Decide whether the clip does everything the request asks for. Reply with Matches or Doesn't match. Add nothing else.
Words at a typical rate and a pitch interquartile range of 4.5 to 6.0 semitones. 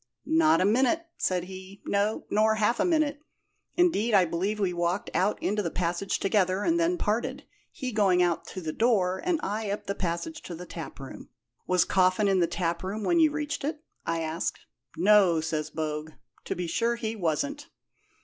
Matches